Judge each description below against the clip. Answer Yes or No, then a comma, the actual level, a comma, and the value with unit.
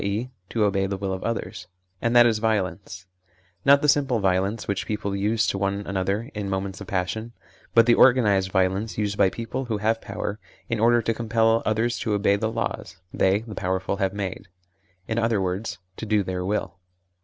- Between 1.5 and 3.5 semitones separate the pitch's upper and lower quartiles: Yes, average, 2.7 semitones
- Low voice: Yes, low, 105 Hz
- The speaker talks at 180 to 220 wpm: Yes, average, 195 wpm